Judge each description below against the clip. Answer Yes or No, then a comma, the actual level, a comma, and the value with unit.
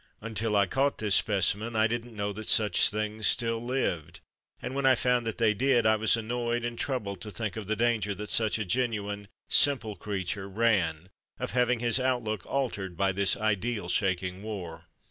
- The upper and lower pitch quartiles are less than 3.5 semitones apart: Yes, average, 2.9 semitones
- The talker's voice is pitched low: Yes, low, 110 Hz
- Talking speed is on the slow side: No, average, 185 wpm